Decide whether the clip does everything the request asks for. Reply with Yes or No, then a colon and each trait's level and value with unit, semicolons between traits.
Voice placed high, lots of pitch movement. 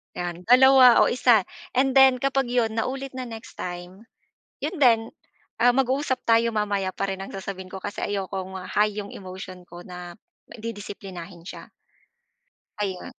No: high, 205 Hz; average, 4.8 semitones